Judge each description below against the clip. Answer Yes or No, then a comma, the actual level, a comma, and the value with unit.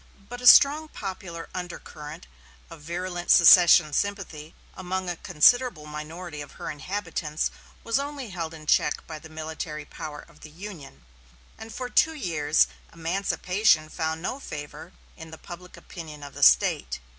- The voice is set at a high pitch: No, medium, 170 Hz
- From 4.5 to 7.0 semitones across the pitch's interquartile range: No, average, 4.0 semitones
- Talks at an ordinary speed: Yes, average, 150 wpm